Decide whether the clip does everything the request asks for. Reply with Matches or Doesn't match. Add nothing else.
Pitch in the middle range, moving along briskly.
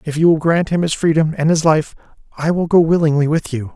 Matches